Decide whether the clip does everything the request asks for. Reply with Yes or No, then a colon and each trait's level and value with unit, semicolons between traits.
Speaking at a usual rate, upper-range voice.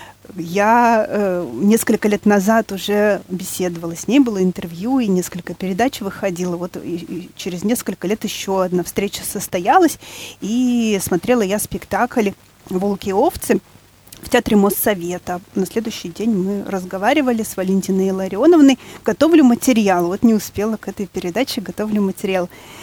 Yes: average, 140 wpm; high, 200 Hz